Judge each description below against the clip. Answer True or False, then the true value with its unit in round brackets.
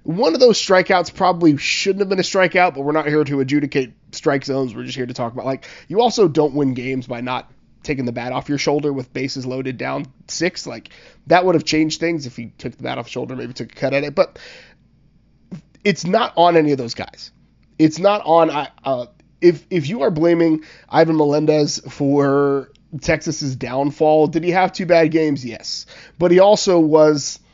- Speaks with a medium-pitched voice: True (150 Hz)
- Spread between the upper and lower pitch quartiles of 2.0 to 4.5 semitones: True (4.2 semitones)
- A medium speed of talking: False (210 wpm)